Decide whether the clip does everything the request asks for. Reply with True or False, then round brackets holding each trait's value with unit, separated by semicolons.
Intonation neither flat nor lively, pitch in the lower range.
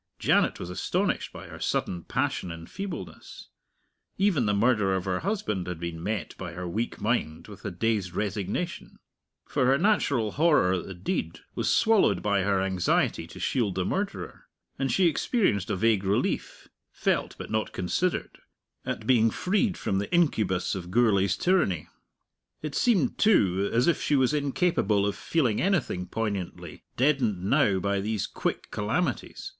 False (7.4 semitones; 105 Hz)